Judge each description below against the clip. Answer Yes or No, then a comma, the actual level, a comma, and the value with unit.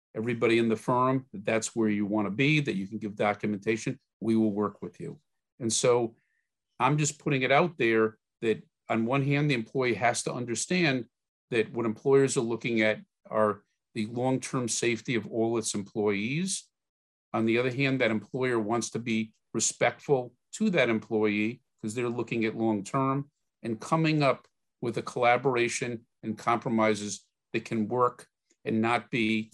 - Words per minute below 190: Yes, average, 175 wpm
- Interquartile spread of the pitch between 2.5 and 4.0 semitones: Yes, average, 3.1 semitones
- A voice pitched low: Yes, low, 115 Hz